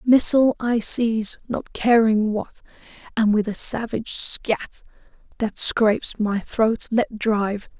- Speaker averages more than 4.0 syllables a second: No, 3.9 syllables/s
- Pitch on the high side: Yes, high, 220 Hz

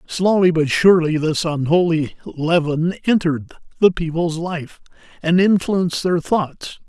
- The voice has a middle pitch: Yes, medium, 170 Hz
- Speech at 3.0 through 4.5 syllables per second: Yes, 4.2 syllables/s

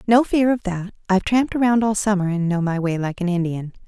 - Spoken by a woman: Yes, female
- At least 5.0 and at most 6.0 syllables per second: Yes, 5.8 syllables/s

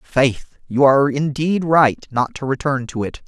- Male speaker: Yes, male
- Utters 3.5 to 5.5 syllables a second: Yes, 4.3 syllables/s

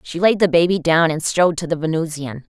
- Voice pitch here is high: No, medium, 165 Hz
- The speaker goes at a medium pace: No, fast, 235 wpm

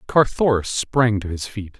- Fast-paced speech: No, average, 165 wpm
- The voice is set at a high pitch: No, low, 110 Hz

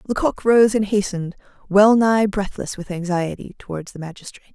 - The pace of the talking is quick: No, average, 160 wpm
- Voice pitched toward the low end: No, high, 200 Hz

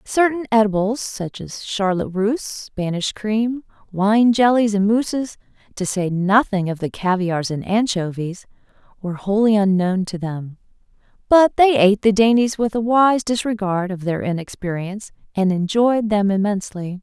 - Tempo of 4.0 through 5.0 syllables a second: Yes, 4.7 syllables/s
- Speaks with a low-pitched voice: No, high, 205 Hz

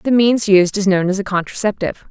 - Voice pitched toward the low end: No, high, 200 Hz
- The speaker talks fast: Yes, fast, 230 wpm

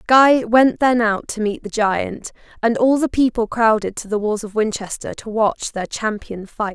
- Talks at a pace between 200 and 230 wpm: Yes, fast, 205 wpm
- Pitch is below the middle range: No, high, 225 Hz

